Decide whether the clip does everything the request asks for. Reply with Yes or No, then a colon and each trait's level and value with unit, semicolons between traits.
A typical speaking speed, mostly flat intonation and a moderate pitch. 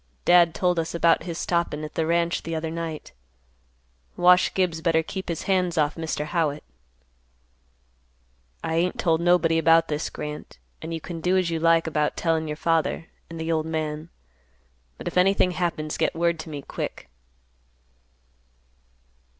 Yes: average, 160 wpm; narrow, 1.3 semitones; medium, 165 Hz